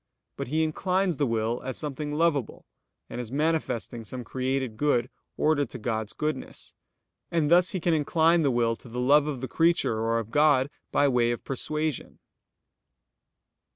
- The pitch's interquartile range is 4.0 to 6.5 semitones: Yes, average, 4.5 semitones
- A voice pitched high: No, medium, 140 Hz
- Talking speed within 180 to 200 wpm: No, average, 165 wpm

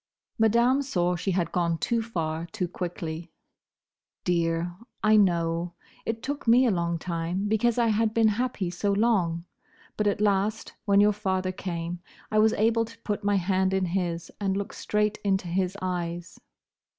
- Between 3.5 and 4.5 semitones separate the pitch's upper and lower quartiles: Yes, average, 3.8 semitones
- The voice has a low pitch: No, high, 190 Hz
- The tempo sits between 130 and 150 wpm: No, average, 165 wpm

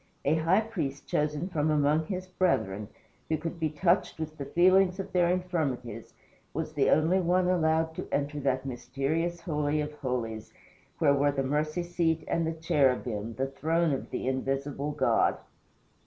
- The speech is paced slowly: No, average, 165 wpm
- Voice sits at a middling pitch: Yes, medium, 155 Hz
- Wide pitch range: No, average, 3.9 semitones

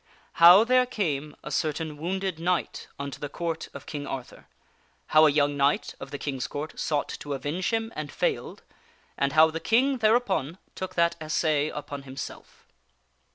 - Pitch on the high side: No, medium, 155 Hz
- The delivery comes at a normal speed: Yes, average, 170 wpm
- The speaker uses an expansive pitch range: No, average, 4.2 semitones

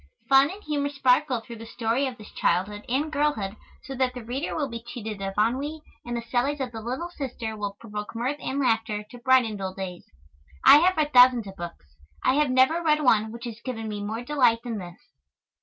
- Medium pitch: No, high, 240 Hz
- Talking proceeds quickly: Yes, fast, 215 wpm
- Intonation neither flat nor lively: Yes, average, 4.0 semitones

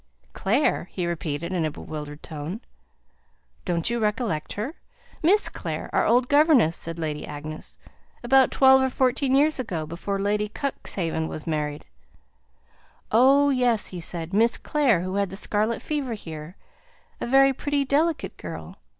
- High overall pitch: Yes, high, 210 Hz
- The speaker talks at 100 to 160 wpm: Yes, average, 150 wpm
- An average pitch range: No, wide, 8.2 semitones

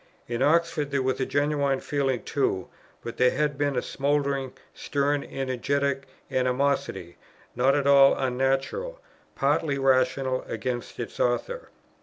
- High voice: No, medium, 140 Hz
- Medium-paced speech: No, slow, 125 wpm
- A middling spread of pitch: No, narrow, 1.7 semitones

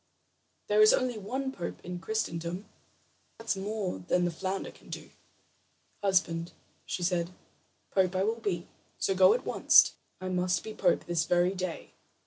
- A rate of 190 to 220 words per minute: No, average, 155 wpm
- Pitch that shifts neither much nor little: Yes, average, 3.0 semitones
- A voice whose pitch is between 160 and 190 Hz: Yes, medium, 185 Hz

